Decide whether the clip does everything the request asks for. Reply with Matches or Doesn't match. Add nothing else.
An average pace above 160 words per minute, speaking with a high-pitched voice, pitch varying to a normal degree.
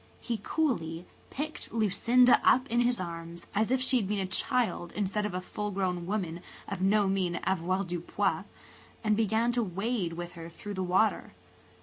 Matches